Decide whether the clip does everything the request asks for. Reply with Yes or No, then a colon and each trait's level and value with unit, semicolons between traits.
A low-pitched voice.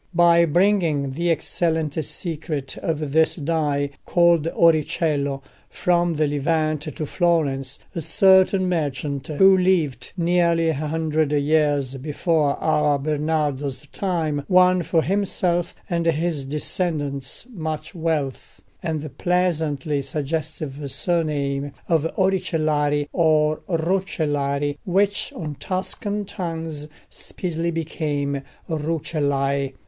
No: medium, 155 Hz